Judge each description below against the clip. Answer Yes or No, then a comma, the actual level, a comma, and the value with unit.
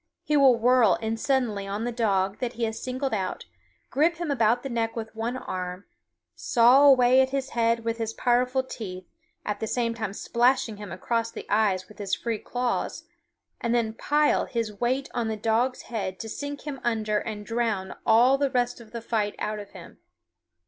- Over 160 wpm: Yes, average, 195 wpm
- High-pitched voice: Yes, high, 230 Hz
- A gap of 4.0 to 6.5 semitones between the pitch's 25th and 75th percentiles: No, average, 2.8 semitones